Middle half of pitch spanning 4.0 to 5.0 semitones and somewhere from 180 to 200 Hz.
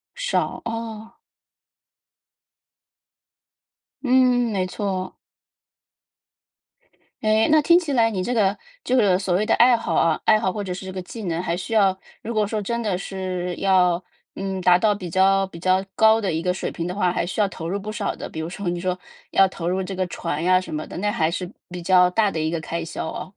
No: average, 3.2 semitones; high, 190 Hz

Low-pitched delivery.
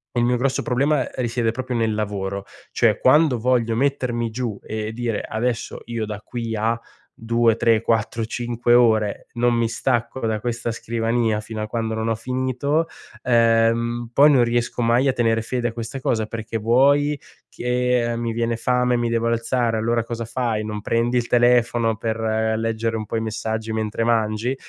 Yes: low, 115 Hz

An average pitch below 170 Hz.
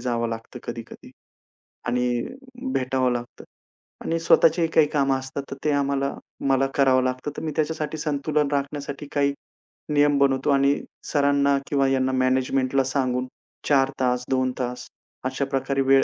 Yes: low, 135 Hz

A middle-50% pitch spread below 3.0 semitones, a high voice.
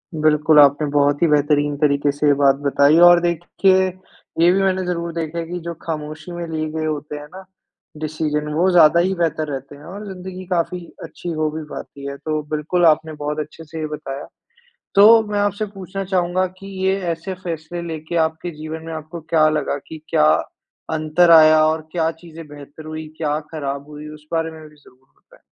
No: narrow, 2.4 semitones; medium, 160 Hz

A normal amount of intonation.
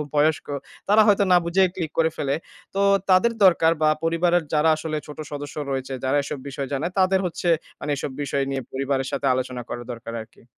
Yes: average, 4.2 semitones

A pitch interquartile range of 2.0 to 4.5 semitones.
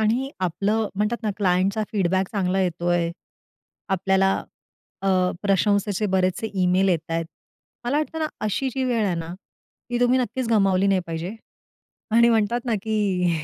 Yes: average, 3.4 semitones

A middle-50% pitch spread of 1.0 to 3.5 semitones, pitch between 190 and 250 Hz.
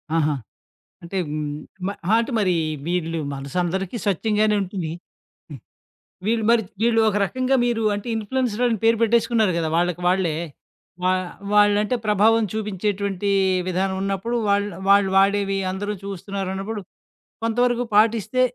Yes: average, 2.9 semitones; high, 205 Hz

